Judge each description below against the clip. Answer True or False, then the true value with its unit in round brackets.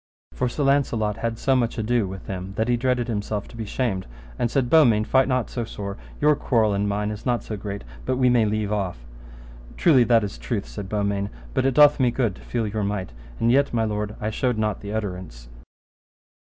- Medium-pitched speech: False (110 Hz)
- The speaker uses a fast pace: True (215 wpm)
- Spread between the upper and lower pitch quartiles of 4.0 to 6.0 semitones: False (3.4 semitones)